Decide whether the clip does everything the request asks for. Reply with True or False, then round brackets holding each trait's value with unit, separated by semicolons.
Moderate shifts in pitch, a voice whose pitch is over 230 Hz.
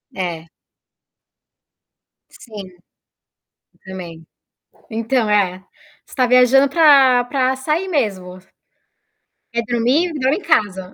False (6.2 semitones; 240 Hz)